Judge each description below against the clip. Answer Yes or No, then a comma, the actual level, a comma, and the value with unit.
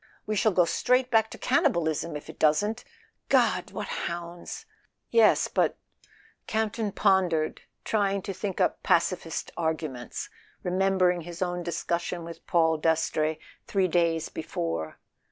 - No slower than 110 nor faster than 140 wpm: Yes, slow, 135 wpm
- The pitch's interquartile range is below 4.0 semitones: Yes, average, 3.5 semitones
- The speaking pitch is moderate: Yes, medium, 175 Hz